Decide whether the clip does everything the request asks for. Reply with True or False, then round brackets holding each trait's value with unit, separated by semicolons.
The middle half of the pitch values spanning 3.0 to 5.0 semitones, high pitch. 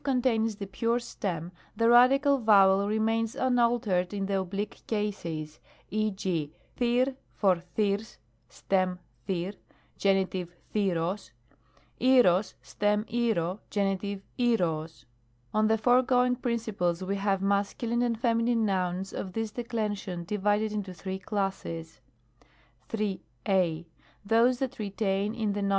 True (3.3 semitones; 205 Hz)